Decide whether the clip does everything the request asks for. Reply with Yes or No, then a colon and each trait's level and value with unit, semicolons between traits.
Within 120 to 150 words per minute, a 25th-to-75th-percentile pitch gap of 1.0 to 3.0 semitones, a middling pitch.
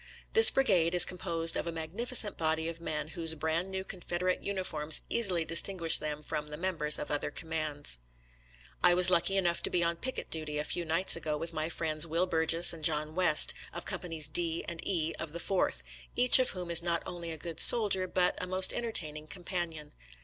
No: average, 200 wpm; narrow, 2.4 semitones; medium, 170 Hz